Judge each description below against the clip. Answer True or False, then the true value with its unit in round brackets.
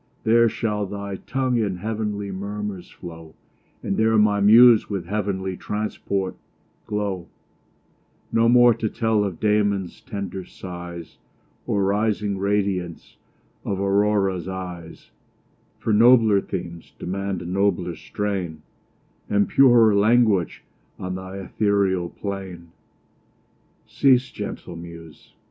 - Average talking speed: False (110 wpm)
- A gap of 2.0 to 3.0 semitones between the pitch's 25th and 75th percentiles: True (2.4 semitones)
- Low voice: True (100 Hz)